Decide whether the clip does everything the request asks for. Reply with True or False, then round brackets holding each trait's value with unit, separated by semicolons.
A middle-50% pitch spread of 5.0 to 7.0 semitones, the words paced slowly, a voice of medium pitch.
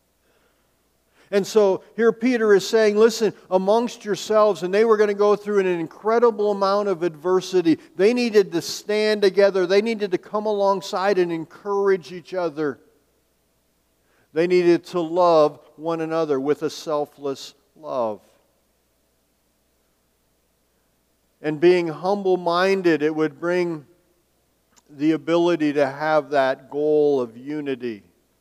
True (5.4 semitones; 125 wpm; 175 Hz)